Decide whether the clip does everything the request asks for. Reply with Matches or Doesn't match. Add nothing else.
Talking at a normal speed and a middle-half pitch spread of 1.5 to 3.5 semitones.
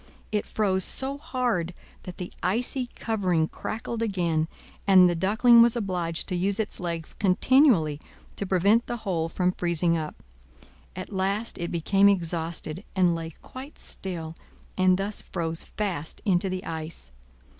Doesn't match